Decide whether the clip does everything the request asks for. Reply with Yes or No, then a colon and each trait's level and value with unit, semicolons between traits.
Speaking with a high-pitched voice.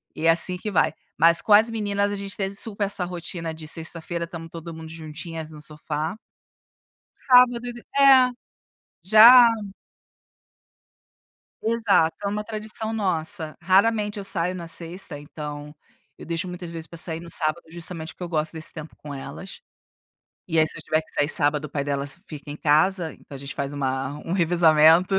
No: medium, 170 Hz